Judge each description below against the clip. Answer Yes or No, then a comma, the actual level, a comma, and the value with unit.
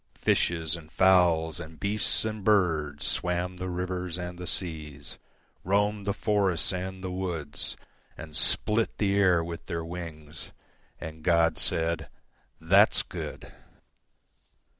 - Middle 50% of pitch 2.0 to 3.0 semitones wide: Yes, narrow, 2.6 semitones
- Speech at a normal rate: No, slow, 105 wpm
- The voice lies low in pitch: Yes, very low, 90 Hz